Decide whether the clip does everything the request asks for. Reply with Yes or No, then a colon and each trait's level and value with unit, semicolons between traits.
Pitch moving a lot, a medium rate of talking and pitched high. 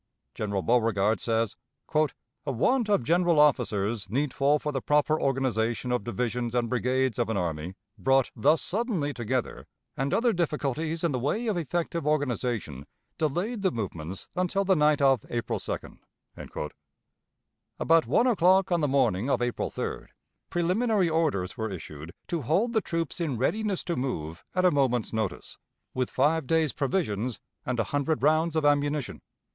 No: wide, 6.0 semitones; average, 155 wpm; medium, 140 Hz